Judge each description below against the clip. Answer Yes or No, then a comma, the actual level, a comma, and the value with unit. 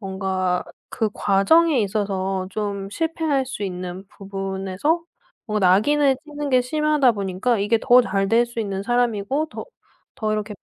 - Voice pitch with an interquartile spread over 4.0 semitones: Yes, average, 5.1 semitones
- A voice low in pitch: No, high, 210 Hz